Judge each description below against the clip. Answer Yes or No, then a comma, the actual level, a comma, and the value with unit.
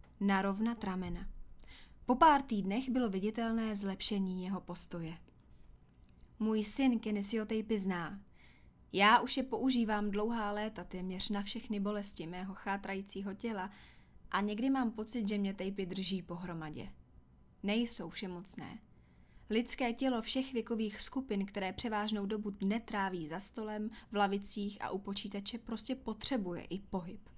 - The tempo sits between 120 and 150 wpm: Yes, average, 135 wpm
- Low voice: No, high, 205 Hz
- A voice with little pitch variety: No, average, 3.2 semitones